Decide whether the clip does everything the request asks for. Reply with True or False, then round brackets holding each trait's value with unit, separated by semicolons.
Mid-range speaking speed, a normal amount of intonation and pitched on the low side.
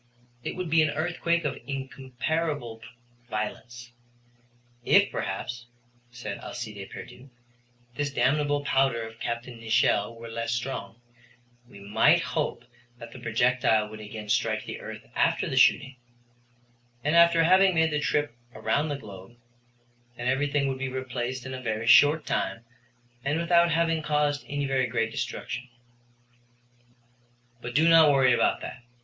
True (145 wpm; 4.1 semitones; 130 Hz)